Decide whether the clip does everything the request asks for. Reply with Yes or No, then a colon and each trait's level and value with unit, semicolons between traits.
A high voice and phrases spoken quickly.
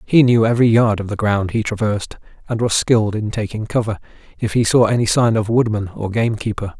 No: low, 110 Hz; fast, 210 wpm